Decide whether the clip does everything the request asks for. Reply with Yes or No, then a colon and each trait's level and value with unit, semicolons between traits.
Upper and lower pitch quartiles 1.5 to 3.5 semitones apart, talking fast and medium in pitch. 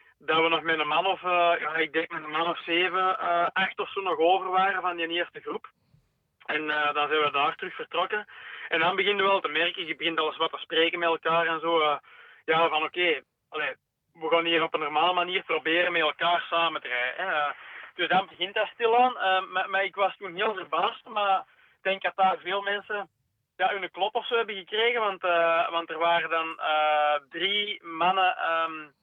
Yes: average, 2.8 semitones; fast, 225 wpm; medium, 170 Hz